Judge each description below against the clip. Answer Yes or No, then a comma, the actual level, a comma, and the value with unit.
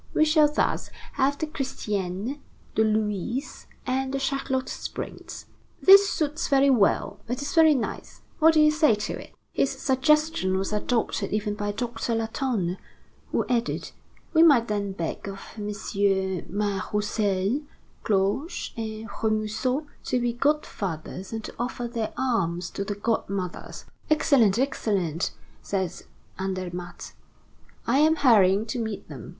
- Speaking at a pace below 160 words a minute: Yes, average, 140 wpm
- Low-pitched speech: No, high, 225 Hz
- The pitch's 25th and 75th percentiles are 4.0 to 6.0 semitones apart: Yes, wide, 5.4 semitones